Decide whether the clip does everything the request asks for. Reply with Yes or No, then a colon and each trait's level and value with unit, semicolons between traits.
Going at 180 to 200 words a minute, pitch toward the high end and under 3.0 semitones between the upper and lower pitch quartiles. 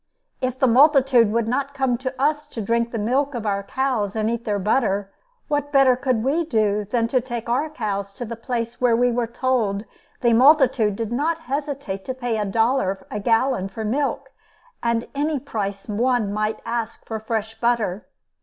No: average, 190 wpm; high, 235 Hz; average, 3.6 semitones